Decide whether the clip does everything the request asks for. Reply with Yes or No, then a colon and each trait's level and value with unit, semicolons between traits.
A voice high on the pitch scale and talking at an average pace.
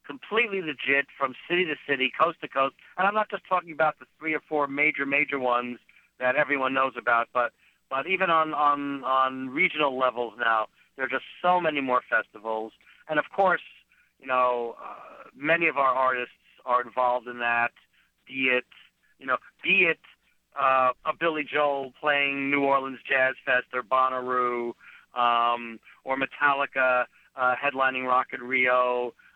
No: low, 130 Hz; average, 165 wpm